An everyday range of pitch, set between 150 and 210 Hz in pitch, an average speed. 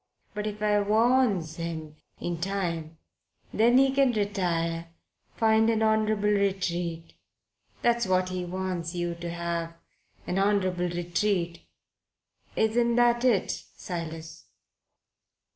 No: average, 4.2 semitones; medium, 185 Hz; slow, 110 wpm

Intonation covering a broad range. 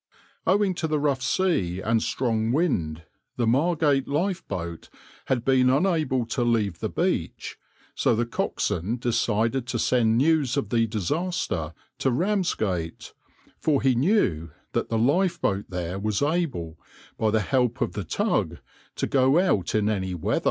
Yes: wide, 6.5 semitones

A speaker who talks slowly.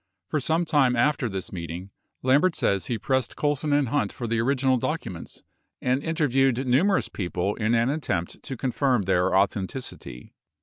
No: average, 165 wpm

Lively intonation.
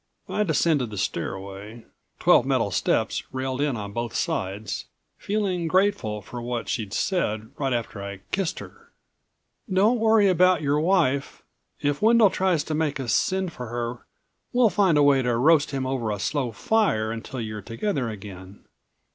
Yes: wide, 8.7 semitones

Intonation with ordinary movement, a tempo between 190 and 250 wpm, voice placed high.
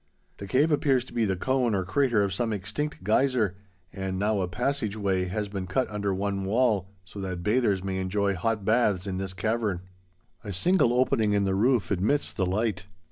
No: average, 3.7 semitones; average, 195 wpm; low, 105 Hz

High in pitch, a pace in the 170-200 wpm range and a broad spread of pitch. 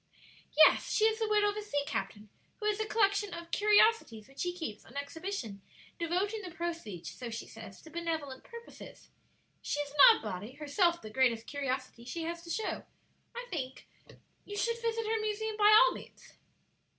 Yes: very high, 340 Hz; average, 185 wpm; wide, 8.3 semitones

